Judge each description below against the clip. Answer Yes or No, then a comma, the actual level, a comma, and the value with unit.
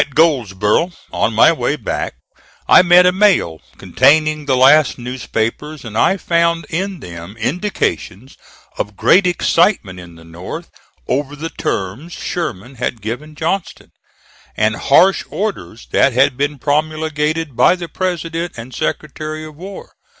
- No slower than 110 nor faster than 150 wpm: Yes, average, 140 wpm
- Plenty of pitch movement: Yes, wide, 6.3 semitones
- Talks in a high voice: No, medium, 150 Hz